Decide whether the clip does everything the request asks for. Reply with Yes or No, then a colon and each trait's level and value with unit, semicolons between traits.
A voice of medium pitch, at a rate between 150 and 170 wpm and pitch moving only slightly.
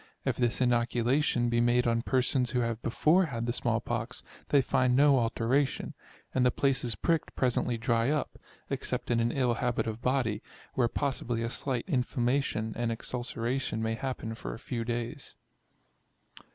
No: low, 120 Hz; average, 165 wpm; narrow, 2.1 semitones